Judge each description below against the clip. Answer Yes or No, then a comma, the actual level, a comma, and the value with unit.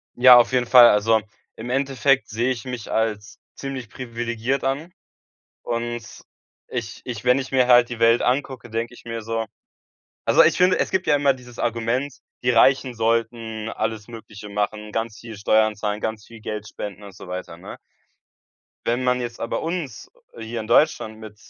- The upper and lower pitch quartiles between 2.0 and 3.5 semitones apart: Yes, narrow, 2.4 semitones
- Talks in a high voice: No, low, 115 Hz